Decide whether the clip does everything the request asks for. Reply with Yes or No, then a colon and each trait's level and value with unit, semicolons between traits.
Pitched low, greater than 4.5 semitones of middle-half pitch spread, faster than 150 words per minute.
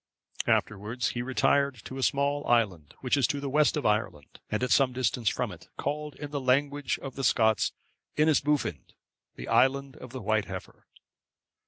No: low, 130 Hz; average, 4.0 semitones; average, 175 wpm